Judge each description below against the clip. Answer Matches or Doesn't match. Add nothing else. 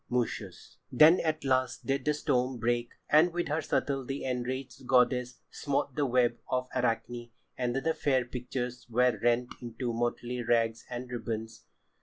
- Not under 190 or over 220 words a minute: Doesn't match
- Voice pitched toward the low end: Matches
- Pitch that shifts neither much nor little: Doesn't match